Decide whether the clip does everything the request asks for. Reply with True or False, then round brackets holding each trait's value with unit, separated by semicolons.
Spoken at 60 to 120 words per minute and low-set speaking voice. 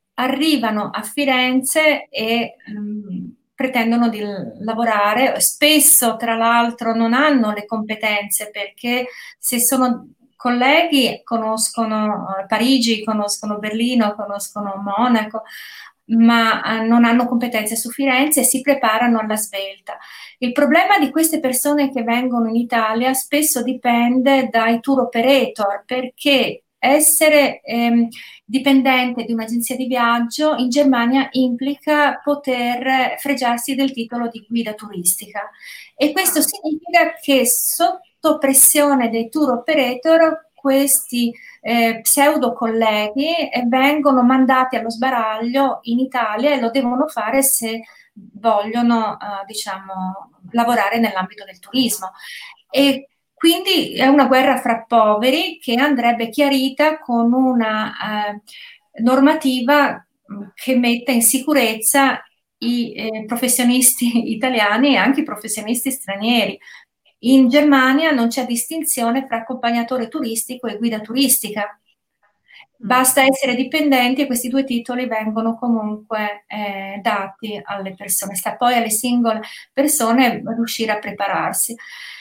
False (115 wpm; 245 Hz)